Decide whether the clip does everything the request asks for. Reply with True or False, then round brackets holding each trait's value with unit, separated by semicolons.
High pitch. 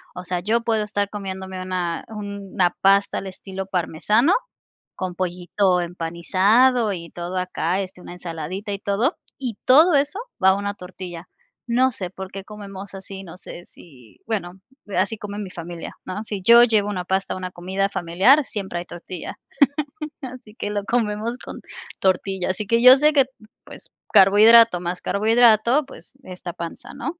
True (195 Hz)